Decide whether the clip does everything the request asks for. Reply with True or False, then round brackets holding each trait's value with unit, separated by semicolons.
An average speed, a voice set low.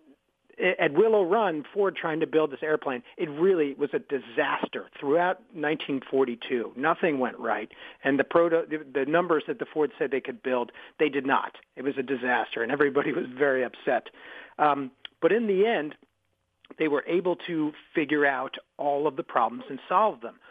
False (180 wpm; 150 Hz)